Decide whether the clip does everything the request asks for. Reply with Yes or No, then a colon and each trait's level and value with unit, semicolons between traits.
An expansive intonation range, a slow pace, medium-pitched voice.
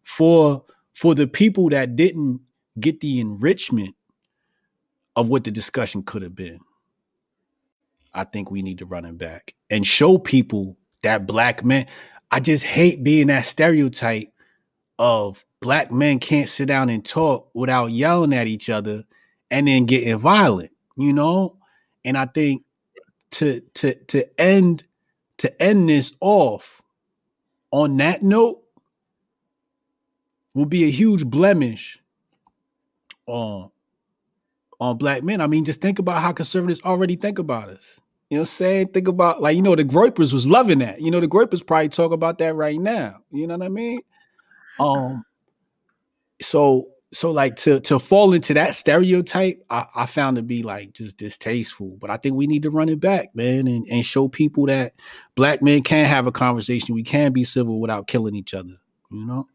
No: wide, 6.3 semitones; average, 170 wpm; medium, 145 Hz